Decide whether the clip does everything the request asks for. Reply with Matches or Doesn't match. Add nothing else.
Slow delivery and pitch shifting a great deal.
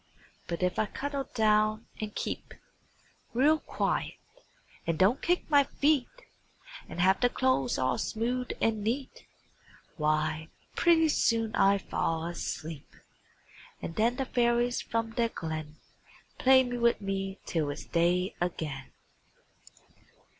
Matches